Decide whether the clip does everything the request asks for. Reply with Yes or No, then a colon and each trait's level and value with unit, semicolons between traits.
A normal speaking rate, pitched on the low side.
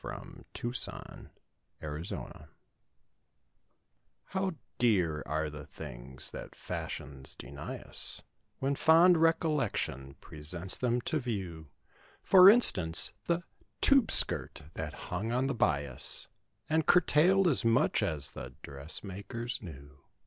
No: slow, 120 wpm; low, 100 Hz